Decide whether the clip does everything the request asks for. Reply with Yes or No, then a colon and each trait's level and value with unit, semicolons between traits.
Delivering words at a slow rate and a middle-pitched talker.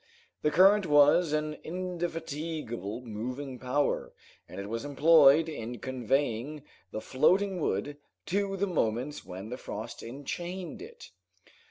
Yes: slow, 125 wpm; medium, 145 Hz